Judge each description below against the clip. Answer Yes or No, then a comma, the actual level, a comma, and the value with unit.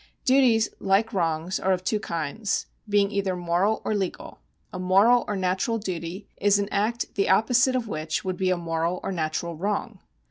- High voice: Yes, high, 195 Hz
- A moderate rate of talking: Yes, average, 180 wpm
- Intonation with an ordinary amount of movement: Yes, average, 3.4 semitones